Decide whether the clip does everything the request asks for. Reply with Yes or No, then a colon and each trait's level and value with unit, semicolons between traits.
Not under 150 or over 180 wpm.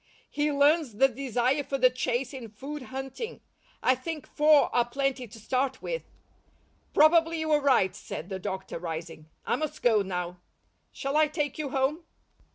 Yes: average, 165 wpm